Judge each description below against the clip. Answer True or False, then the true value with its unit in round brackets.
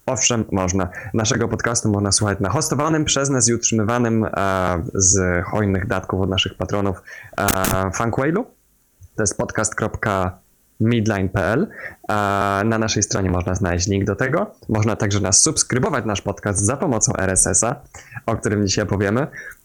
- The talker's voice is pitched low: True (105 Hz)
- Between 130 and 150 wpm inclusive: True (140 wpm)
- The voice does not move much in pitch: False (3.3 semitones)